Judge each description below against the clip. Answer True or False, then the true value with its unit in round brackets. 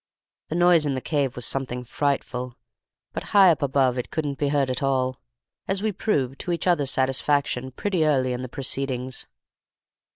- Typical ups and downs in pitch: True (3.1 semitones)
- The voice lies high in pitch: False (135 Hz)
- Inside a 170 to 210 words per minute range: True (175 wpm)